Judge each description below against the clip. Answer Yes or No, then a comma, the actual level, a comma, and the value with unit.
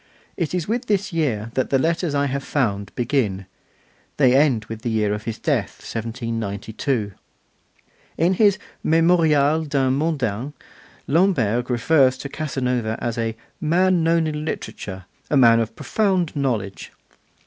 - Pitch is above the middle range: No, low, 135 Hz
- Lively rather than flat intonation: Yes, wide, 5.8 semitones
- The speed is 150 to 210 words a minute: No, average, 140 wpm